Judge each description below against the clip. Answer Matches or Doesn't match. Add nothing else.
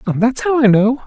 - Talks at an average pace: Doesn't match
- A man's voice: Matches